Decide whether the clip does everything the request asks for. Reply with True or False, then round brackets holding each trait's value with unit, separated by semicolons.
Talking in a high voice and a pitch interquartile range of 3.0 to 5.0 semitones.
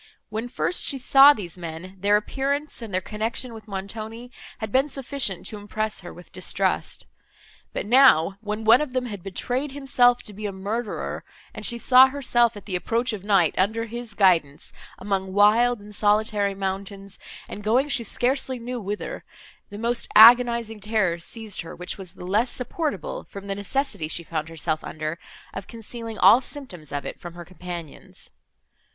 True (215 Hz; 4.2 semitones)